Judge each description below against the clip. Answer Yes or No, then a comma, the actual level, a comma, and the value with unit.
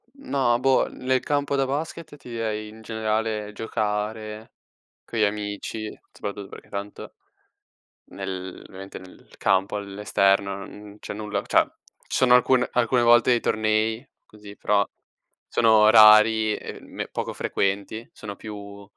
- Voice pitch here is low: Yes, low, 110 Hz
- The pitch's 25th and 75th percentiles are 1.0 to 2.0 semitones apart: No, narrow, 2.4 semitones